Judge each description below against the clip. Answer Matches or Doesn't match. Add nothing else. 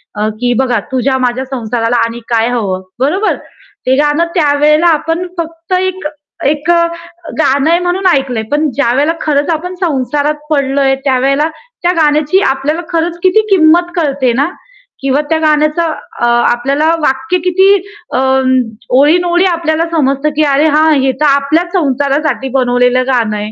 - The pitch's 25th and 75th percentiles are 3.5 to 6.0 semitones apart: Matches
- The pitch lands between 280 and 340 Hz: Matches